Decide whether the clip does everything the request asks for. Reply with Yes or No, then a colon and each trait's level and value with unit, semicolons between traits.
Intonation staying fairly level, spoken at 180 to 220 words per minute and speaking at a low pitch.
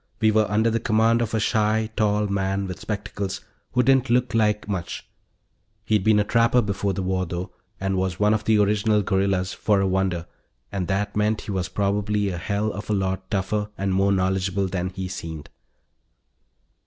Yes: narrow, 2.1 semitones; average, 190 wpm; low, 100 Hz